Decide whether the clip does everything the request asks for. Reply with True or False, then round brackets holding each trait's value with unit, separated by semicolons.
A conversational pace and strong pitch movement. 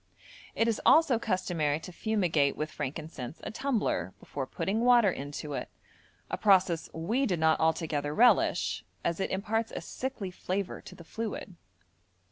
True (150 wpm; 6.2 semitones)